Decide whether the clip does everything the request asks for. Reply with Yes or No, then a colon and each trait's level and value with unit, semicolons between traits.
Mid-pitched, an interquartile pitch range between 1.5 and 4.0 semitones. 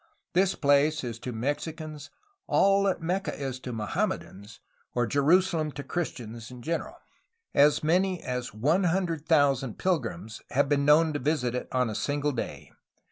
No: medium, 145 Hz; average, 4.6 semitones